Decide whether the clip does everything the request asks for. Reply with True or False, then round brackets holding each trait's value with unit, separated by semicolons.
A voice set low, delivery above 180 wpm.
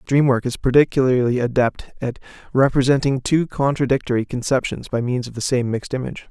False (130 Hz; 170 wpm)